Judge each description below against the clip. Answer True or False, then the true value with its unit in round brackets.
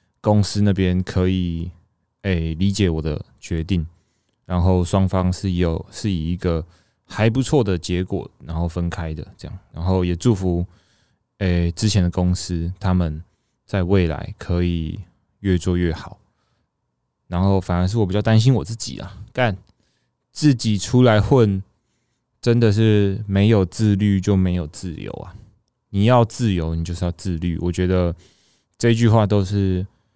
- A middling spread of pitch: True (3.4 semitones)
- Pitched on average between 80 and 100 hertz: True (95 Hz)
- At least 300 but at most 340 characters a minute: False (220 characters per minute)